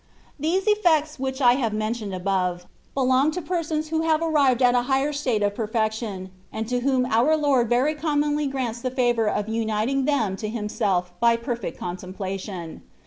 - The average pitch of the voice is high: Yes, high, 245 Hz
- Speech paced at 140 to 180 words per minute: Yes, average, 170 wpm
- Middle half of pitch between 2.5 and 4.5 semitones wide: No, wide, 5.4 semitones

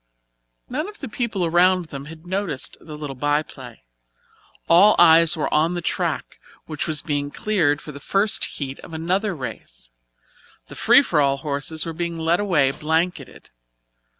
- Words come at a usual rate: Yes, average, 165 wpm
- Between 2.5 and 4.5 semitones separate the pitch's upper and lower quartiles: Yes, average, 3.6 semitones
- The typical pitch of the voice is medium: Yes, medium, 160 Hz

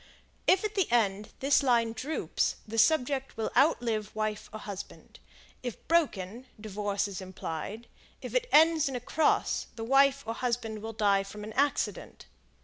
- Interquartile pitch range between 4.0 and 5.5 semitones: Yes, average, 4.7 semitones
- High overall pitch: Yes, high, 230 Hz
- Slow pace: No, average, 160 wpm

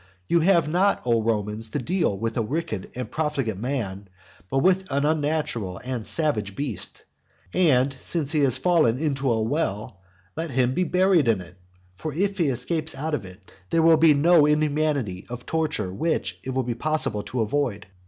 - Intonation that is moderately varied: No, wide, 5.9 semitones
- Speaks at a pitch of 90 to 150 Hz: Yes, medium, 140 Hz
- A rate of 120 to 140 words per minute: No, average, 185 wpm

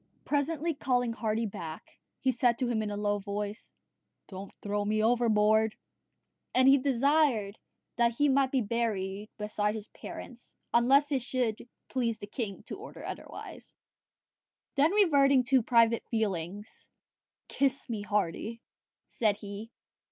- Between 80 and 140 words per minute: Yes, slow, 135 wpm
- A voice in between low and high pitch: No, high, 230 Hz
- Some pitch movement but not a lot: Yes, average, 3.9 semitones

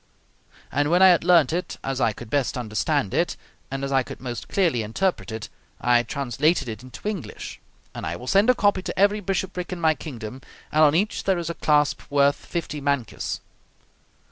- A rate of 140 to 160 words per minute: No, average, 195 wpm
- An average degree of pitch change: No, wide, 6.4 semitones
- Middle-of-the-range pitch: Yes, medium, 145 Hz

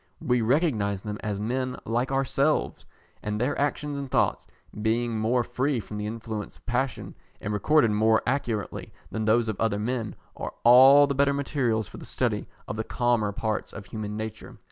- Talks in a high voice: No, low, 115 Hz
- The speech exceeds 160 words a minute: Yes, average, 180 wpm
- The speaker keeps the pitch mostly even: No, average, 3.5 semitones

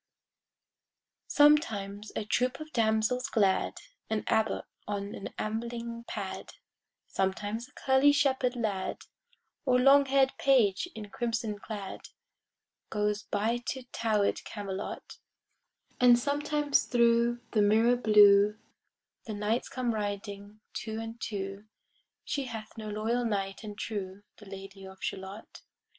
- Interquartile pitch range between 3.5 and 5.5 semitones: No, average, 3.1 semitones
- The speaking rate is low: Yes, slow, 120 wpm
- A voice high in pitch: Yes, high, 220 Hz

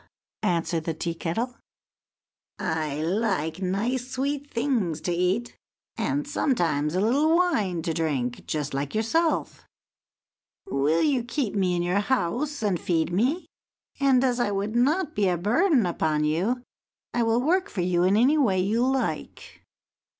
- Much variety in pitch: Yes, wide, 7.2 semitones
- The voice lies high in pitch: Yes, high, 205 Hz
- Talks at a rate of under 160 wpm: Yes, average, 150 wpm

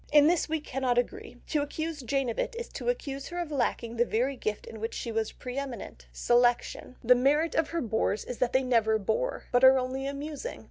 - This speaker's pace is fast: Yes, fast, 220 wpm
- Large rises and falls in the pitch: No, average, 3.8 semitones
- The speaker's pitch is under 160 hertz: No, very high, 260 Hz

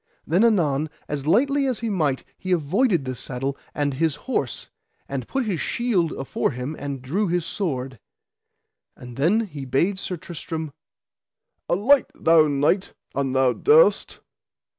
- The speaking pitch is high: No, medium, 160 Hz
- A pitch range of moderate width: No, wide, 6.6 semitones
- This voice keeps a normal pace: Yes, average, 145 wpm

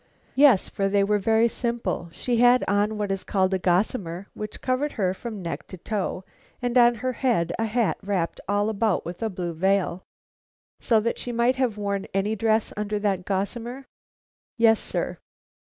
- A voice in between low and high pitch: No, high, 210 Hz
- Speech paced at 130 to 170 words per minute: No, average, 180 wpm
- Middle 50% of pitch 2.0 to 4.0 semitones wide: Yes, average, 3.5 semitones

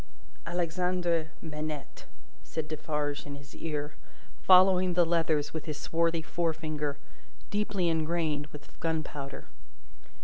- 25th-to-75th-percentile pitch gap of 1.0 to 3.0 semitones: Yes, narrow, 2.4 semitones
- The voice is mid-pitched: Yes, medium, 160 Hz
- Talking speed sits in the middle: No, slow, 105 wpm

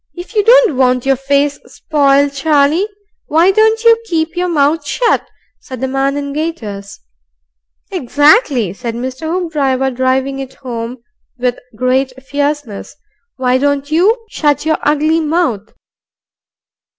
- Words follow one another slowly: Yes, slow, 130 wpm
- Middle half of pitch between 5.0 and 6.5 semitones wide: No, average, 3.8 semitones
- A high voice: Yes, very high, 285 Hz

